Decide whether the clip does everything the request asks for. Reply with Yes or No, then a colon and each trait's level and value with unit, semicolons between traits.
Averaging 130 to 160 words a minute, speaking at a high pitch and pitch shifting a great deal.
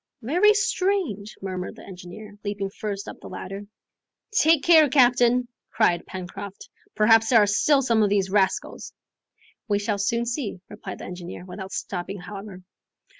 No: average, 150 wpm; high, 205 Hz; average, 3.9 semitones